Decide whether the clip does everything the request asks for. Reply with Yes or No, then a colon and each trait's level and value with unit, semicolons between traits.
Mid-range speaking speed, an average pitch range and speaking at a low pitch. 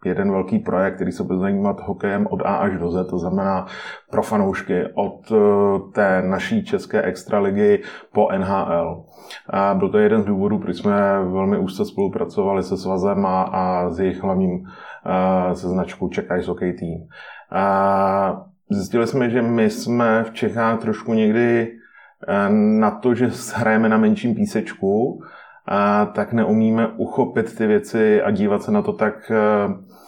Yes: average, 155 wpm; average, 4.3 semitones; low, 110 Hz